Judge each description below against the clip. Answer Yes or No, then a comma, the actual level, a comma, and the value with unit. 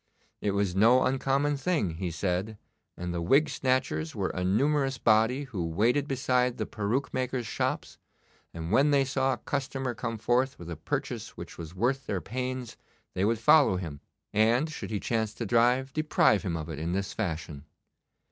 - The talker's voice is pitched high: No, low, 115 Hz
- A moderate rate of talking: Yes, average, 180 wpm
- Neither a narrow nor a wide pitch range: No, wide, 6.2 semitones